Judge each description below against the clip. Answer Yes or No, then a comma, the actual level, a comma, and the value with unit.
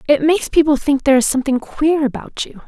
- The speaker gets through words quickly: Yes, fast, 225 wpm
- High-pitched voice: Yes, very high, 285 Hz